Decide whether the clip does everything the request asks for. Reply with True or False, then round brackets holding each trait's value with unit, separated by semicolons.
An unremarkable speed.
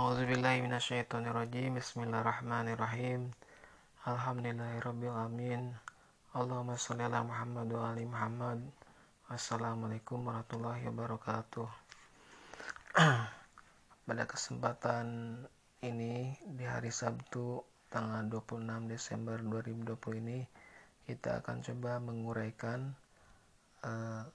False (70 wpm)